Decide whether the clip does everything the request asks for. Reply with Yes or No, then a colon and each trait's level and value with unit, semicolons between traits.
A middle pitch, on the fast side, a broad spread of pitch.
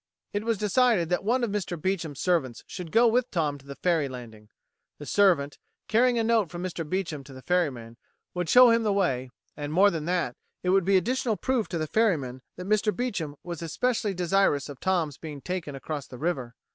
Yes: medium, 175 Hz; fast, 210 wpm; wide, 6.1 semitones